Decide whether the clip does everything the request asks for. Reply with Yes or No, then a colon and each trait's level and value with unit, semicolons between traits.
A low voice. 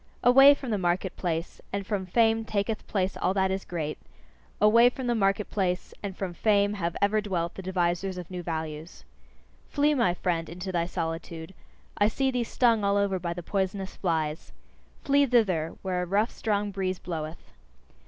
No: high, 190 Hz